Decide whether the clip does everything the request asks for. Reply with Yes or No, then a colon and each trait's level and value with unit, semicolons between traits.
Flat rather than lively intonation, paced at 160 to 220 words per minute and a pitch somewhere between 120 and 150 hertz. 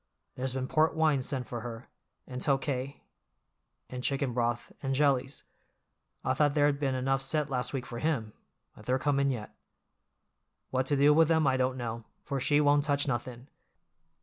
Yes: narrow, 2.3 semitones; average, 170 wpm; low, 135 Hz